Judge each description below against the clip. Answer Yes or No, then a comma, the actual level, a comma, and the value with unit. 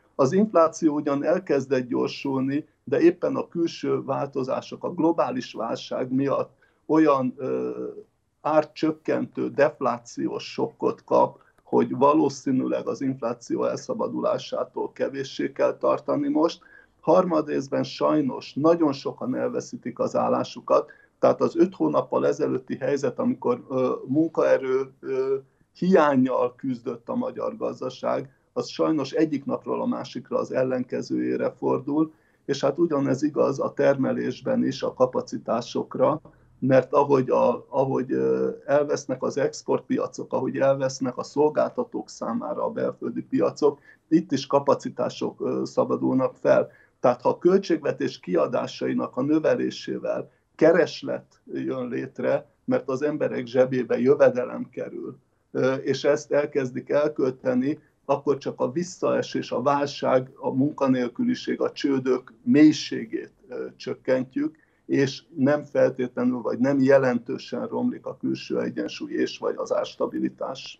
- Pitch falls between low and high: Yes, medium, 150 Hz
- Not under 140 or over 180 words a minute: No, average, 115 wpm